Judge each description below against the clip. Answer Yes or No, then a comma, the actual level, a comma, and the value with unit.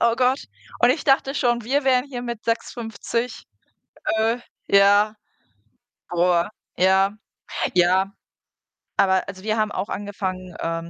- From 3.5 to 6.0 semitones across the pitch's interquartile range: Yes, average, 4.1 semitones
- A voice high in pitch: Yes, high, 210 Hz